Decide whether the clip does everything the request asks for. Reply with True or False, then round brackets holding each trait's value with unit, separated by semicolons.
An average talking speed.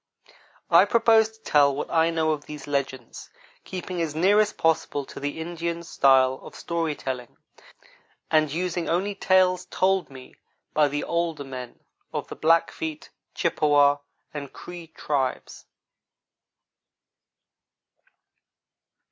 False (120 wpm)